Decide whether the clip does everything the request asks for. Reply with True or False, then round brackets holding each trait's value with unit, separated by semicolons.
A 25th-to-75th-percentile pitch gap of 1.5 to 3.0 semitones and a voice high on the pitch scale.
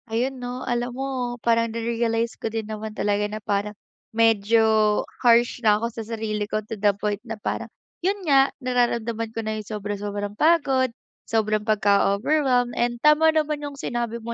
True (2.5 semitones; 230 Hz)